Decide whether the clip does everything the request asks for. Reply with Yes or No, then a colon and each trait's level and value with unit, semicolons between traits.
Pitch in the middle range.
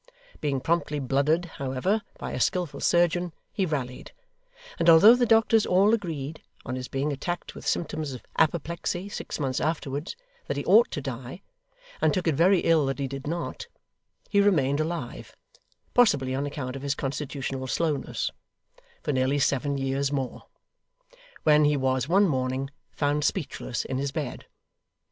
Yes: medium, 145 Hz